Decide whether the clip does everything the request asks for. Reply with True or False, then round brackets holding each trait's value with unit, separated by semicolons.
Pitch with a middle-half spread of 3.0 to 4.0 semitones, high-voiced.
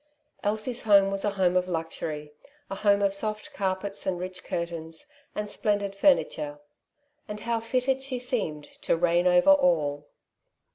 True (3.7 semitones; 195 Hz)